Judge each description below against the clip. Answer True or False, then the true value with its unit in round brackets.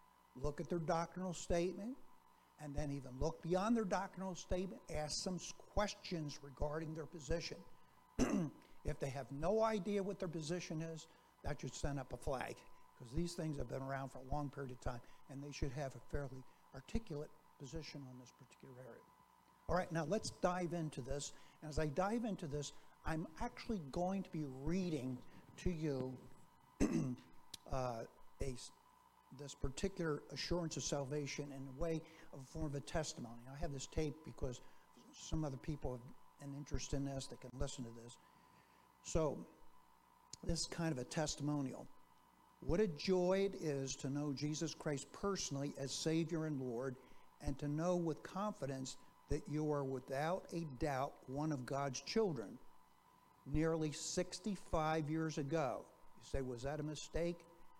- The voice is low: False (150 Hz)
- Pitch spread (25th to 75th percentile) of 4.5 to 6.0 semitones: False (3.8 semitones)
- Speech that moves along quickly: False (165 wpm)